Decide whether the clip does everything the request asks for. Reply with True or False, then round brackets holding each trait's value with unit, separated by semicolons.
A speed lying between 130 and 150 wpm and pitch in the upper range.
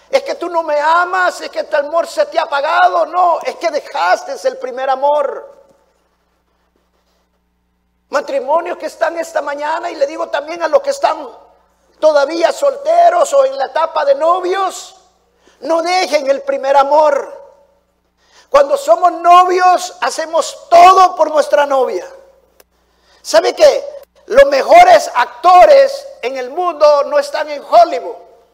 True (140 wpm; 310 Hz)